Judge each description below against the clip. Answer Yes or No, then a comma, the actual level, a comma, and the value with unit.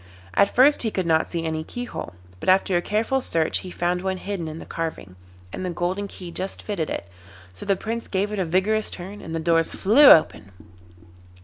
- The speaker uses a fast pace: Yes, fast, 210 wpm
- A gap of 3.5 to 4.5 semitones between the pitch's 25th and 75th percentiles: Yes, average, 3.8 semitones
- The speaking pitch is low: No, medium, 185 Hz